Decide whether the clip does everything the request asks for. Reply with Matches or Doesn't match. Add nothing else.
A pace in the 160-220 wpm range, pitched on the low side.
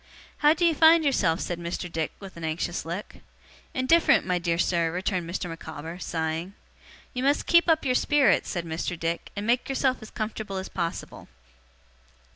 Doesn't match